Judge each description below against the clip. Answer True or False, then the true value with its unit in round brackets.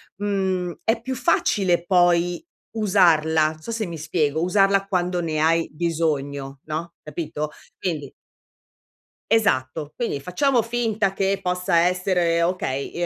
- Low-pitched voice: False (175 Hz)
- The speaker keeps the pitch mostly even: False (3.8 semitones)